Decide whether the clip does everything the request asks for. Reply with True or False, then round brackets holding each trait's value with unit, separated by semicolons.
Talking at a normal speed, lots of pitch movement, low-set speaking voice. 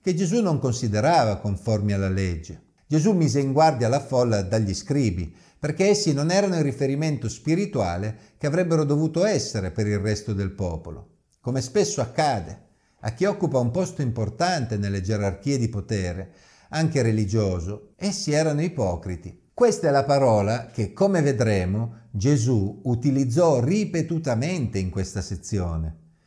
True (140 wpm; 7.4 semitones; 120 Hz)